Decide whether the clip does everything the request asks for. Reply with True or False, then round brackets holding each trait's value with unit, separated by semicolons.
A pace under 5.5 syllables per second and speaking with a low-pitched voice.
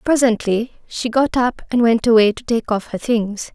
False (4.7 syllables/s; 230 Hz)